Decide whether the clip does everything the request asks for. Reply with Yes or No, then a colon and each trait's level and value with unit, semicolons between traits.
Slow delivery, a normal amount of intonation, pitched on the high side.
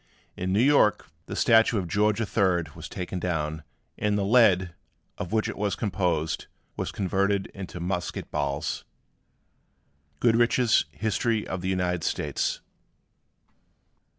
No: slow, 125 wpm; average, 3.3 semitones; very low, 95 Hz